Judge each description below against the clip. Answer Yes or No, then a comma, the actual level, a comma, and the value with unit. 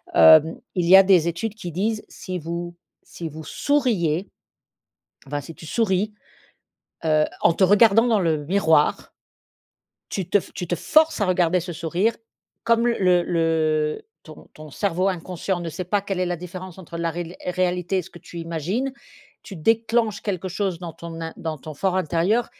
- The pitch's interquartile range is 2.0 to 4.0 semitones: Yes, average, 3.3 semitones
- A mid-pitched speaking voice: Yes, medium, 180 Hz